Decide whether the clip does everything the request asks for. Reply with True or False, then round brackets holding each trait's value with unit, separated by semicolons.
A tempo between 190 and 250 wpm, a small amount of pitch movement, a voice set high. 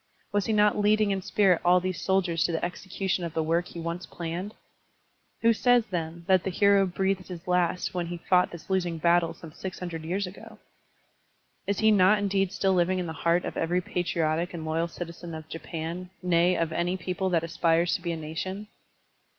False (200 wpm; 2.2 semitones; 180 Hz)